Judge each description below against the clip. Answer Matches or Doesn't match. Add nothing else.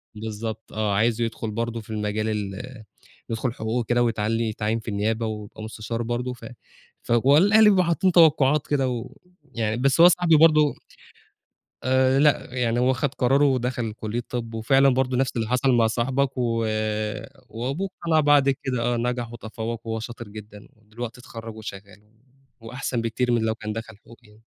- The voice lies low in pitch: Matches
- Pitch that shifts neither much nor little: Matches